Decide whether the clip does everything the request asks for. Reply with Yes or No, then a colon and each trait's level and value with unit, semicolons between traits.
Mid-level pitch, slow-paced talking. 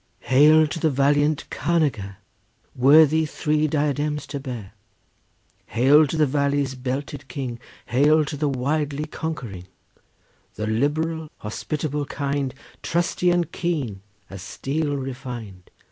Yes: medium, 145 Hz; slow, 115 wpm